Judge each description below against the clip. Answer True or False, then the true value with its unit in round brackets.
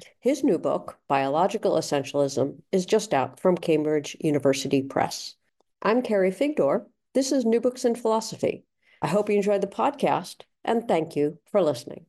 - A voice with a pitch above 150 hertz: True (190 Hz)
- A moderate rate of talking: True (160 wpm)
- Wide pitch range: True (7.8 semitones)